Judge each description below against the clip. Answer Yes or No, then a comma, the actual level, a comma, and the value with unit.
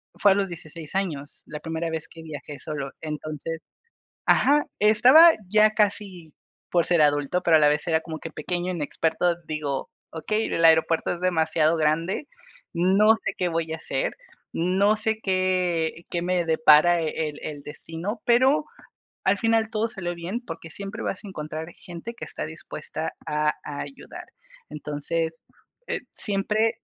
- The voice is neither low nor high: Yes, medium, 170 Hz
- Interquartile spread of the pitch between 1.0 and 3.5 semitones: No, average, 4.0 semitones